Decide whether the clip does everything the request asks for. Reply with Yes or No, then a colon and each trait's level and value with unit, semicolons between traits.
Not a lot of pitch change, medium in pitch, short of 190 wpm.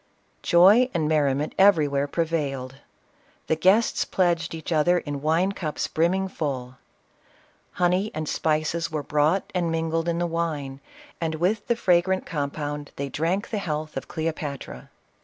No: average, 3.1 semitones; medium, 160 Hz; average, 150 wpm